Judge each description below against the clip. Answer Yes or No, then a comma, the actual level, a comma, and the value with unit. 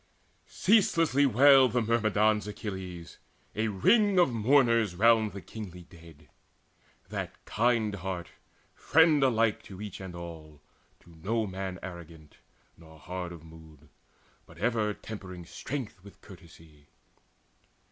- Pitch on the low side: Yes, low, 100 Hz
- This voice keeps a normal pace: No, slow, 120 wpm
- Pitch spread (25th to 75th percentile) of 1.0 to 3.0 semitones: No, average, 5.2 semitones